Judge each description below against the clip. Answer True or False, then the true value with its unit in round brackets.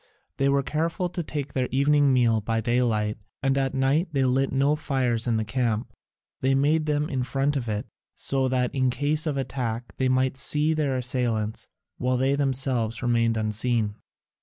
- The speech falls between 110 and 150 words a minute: False (180 wpm)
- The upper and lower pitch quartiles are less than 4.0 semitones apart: True (2.8 semitones)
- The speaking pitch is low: True (130 Hz)